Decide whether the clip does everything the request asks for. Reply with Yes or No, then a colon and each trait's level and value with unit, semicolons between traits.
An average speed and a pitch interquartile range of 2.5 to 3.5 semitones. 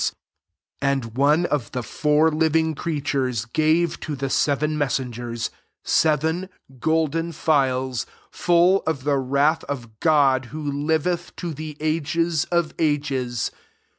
No: slow, 125 wpm; average, 3.0 semitones